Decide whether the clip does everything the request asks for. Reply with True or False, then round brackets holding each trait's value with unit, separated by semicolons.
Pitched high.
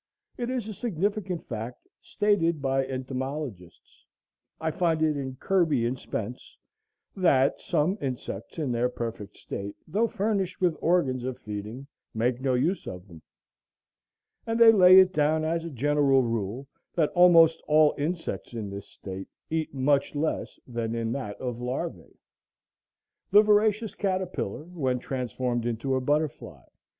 False (140 Hz)